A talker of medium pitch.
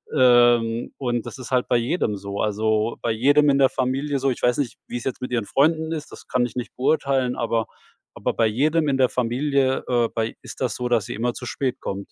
No: low, 125 Hz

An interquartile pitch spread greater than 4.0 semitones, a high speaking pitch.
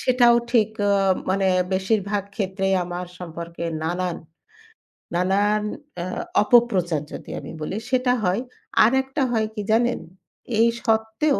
Yes: average, 4.5 semitones; high, 205 Hz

